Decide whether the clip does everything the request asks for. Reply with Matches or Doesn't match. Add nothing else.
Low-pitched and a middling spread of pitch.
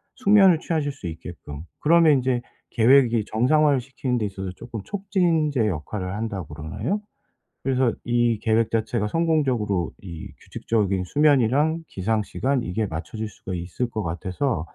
Doesn't match